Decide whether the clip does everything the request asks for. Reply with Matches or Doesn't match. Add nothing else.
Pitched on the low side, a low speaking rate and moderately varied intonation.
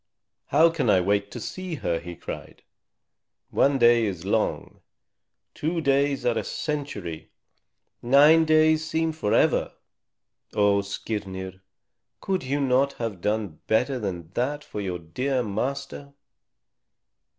Doesn't match